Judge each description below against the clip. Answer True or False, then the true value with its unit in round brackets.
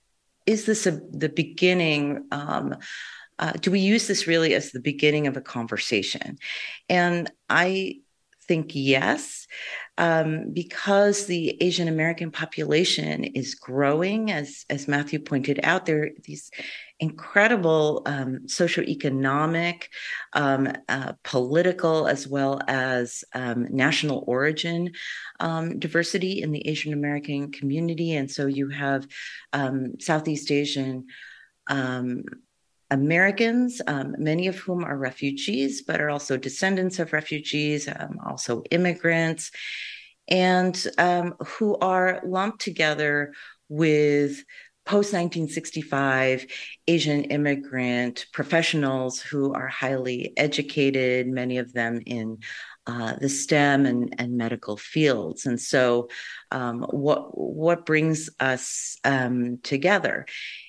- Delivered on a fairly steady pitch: False (3.8 semitones)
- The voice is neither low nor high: True (150 Hz)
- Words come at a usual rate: False (115 wpm)